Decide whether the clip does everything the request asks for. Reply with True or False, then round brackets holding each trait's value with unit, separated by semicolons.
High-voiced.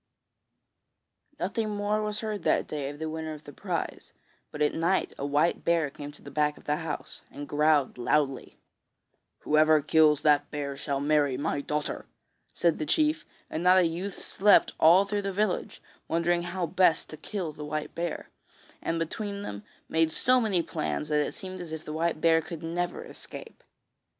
False (160 Hz)